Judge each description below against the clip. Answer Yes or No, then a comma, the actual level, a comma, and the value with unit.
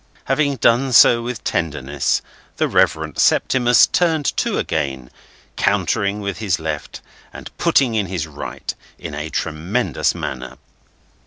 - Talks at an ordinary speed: No, slow, 130 wpm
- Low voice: Yes, very low, 95 Hz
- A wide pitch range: Yes, wide, 8.3 semitones